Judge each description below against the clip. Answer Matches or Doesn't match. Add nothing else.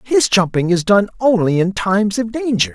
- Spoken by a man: Matches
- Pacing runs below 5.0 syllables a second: Doesn't match